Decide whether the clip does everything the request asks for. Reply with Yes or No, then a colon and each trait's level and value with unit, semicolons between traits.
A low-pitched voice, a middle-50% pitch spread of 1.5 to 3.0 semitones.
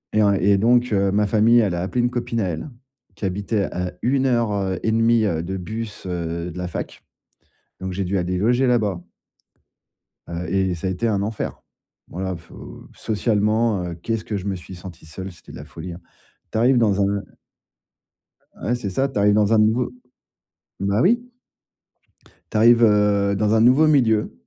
No: low, 105 Hz; average, 3.6 semitones